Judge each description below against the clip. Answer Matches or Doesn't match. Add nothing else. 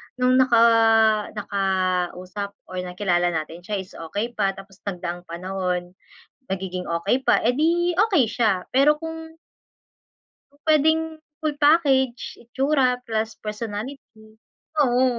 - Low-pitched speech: Doesn't match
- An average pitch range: Doesn't match